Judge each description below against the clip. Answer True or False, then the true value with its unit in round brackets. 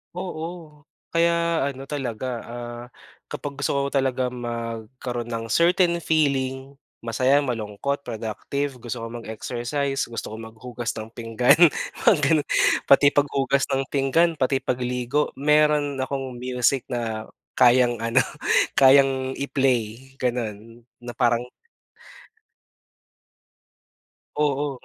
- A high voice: False (130 Hz)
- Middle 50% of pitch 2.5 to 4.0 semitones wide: True (2.9 semitones)